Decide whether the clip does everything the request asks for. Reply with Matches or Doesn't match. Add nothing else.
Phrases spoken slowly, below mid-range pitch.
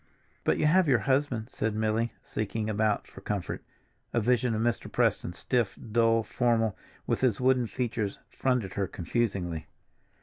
Doesn't match